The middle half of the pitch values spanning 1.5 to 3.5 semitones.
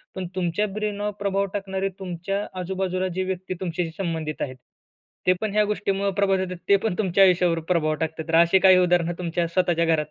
Yes: narrow, 2.5 semitones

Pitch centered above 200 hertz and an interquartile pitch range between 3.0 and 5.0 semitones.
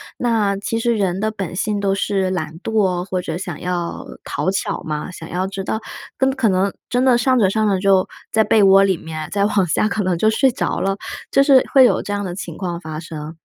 No: high, 195 Hz; average, 3.3 semitones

